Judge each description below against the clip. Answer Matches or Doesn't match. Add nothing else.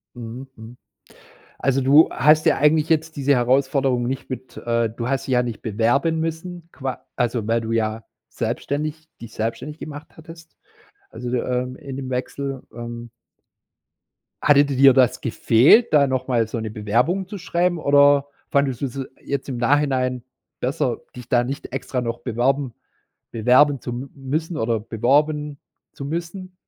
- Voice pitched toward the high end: Doesn't match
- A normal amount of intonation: Matches